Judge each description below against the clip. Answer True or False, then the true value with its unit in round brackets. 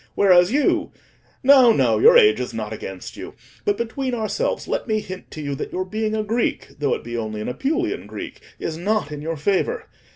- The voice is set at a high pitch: True (215 Hz)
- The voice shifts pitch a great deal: True (8.7 semitones)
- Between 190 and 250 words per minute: True (200 wpm)